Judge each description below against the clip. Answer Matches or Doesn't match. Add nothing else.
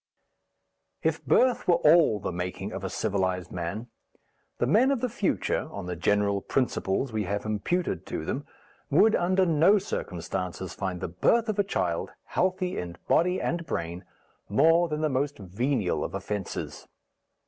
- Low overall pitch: Matches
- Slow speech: Doesn't match